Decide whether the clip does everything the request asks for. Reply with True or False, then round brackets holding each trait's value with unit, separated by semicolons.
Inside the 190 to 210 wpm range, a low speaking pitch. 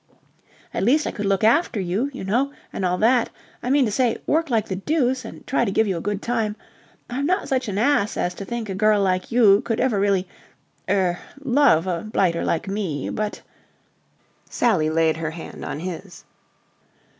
False (195 wpm; 210 Hz)